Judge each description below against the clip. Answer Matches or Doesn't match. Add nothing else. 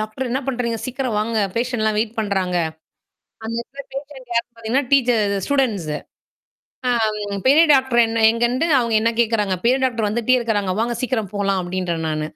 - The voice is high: Matches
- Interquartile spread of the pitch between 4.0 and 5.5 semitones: Doesn't match